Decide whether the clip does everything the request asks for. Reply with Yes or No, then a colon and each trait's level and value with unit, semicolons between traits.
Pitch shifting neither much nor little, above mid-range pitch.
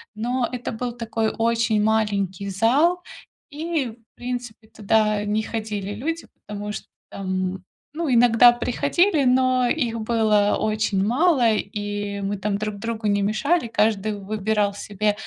Yes: average, 3.0 semitones; high, 220 Hz